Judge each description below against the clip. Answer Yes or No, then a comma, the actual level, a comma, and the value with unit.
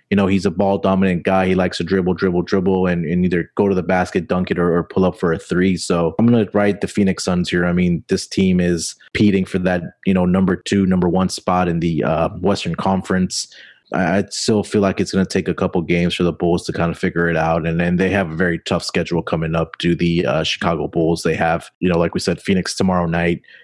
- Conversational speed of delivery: No, fast, 265 wpm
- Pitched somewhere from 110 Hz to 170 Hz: No, very low, 90 Hz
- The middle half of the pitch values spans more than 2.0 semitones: No, narrow, 1.7 semitones